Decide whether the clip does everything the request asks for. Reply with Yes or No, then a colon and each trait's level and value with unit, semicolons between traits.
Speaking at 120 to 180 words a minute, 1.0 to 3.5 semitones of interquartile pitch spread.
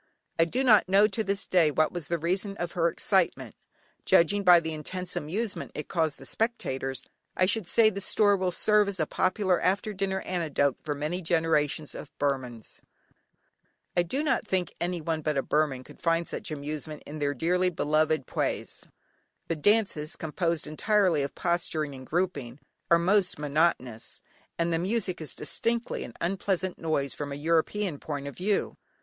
No: average, 170 wpm; average, 4.1 semitones